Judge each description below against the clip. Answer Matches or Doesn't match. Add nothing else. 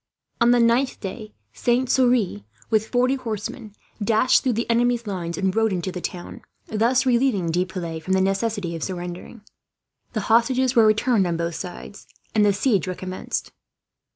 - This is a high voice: Matches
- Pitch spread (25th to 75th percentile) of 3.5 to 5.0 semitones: Matches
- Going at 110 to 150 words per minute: Doesn't match